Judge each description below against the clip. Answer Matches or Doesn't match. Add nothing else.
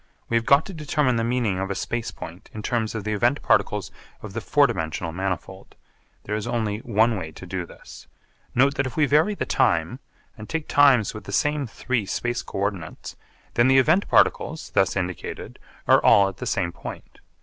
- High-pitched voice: Doesn't match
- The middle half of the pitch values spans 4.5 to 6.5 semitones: Matches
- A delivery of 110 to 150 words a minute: Doesn't match